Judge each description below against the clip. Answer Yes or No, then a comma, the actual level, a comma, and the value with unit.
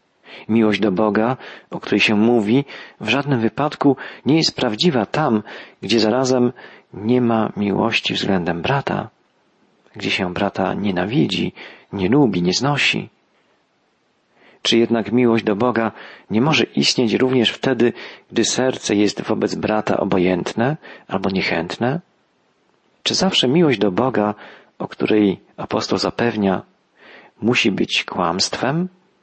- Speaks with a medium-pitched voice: No, low, 115 Hz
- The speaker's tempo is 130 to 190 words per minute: No, average, 120 wpm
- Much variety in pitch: No, average, 3.7 semitones